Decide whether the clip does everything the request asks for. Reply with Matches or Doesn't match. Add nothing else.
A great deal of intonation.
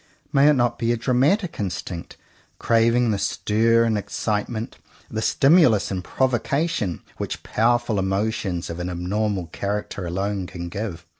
Doesn't match